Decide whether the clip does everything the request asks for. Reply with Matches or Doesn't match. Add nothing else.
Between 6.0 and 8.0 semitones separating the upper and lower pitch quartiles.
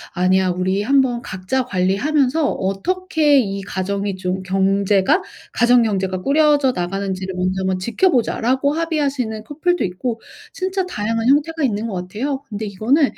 Matches